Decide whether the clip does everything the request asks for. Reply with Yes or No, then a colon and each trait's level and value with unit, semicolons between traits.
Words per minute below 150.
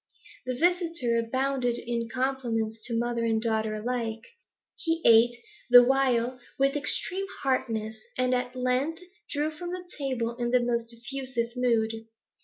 Yes: average, 140 wpm